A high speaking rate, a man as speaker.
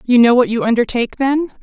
No: fast, 220 wpm; female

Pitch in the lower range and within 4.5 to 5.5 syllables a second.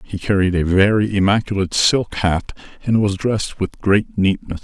Yes: low, 100 Hz; 5.2 syllables/s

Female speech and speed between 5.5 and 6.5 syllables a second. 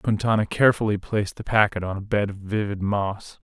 No: male; 5.6 syllables/s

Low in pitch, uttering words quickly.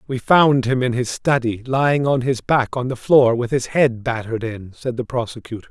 Yes: low, 125 Hz; fast, 220 wpm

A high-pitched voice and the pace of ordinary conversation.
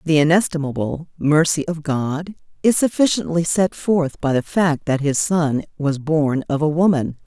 No: medium, 160 Hz; average, 165 wpm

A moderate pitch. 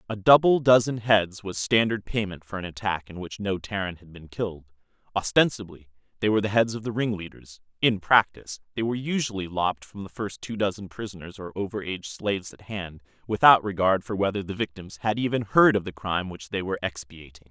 No: low, 100 Hz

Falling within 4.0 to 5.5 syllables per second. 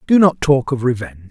No: 6.6 syllables/s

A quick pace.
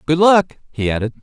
No: average, 195 wpm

